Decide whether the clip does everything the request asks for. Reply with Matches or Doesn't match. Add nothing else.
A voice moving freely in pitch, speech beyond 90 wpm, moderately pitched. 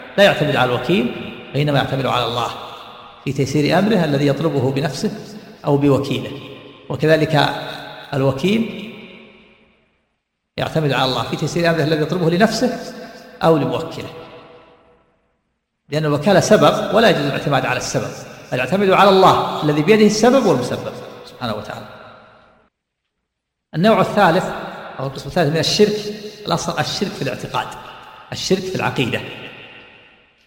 Matches